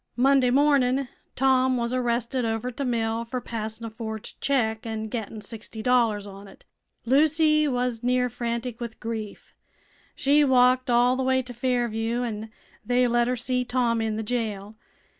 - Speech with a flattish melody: Yes, narrow, 2.2 semitones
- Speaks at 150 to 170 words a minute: Yes, average, 165 wpm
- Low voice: No, high, 240 Hz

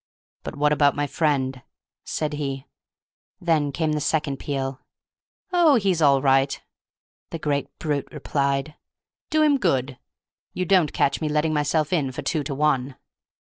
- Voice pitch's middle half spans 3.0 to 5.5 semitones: No, narrow, 2.4 semitones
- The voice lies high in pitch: No, medium, 150 Hz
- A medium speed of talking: Yes, average, 155 wpm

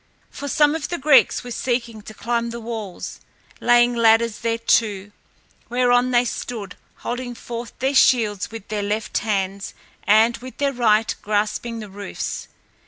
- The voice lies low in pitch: No, high, 230 Hz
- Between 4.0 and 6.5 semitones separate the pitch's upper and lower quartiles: No, narrow, 2.4 semitones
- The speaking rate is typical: Yes, average, 150 wpm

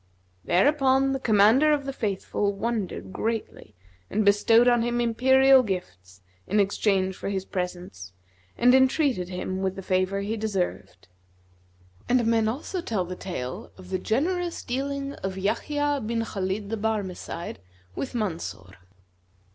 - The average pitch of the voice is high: Yes, high, 215 Hz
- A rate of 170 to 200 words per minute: No, average, 140 wpm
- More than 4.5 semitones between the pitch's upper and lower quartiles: Yes, wide, 5.5 semitones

